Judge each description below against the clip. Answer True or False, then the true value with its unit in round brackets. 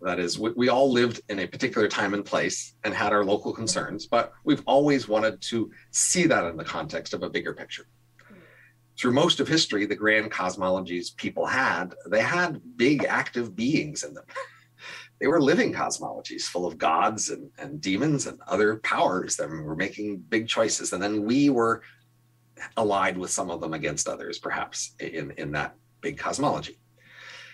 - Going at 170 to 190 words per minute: True (175 wpm)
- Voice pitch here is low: True (110 Hz)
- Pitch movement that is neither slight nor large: True (3.2 semitones)